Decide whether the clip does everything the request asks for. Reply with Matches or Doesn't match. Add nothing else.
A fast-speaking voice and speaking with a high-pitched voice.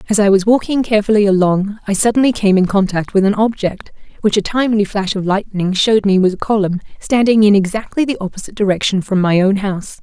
Matches